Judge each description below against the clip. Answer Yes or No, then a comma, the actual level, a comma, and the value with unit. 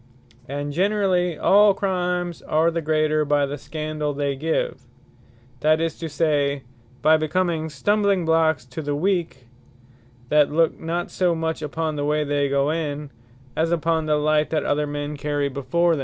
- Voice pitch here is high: No, medium, 155 Hz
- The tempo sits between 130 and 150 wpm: No, average, 165 wpm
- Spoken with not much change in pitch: Yes, narrow, 2.3 semitones